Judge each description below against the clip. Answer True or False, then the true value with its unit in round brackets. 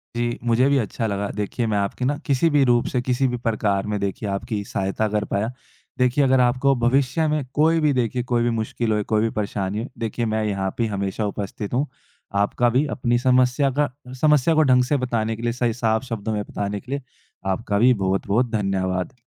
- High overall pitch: False (120 Hz)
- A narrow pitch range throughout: False (3.7 semitones)